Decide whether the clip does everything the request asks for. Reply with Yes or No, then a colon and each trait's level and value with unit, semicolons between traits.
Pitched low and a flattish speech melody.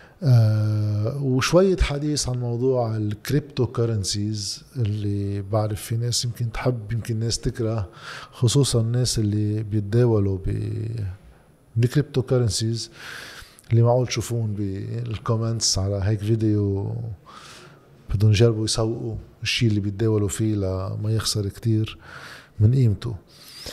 Yes: low, 110 Hz; narrow, 2.3 semitones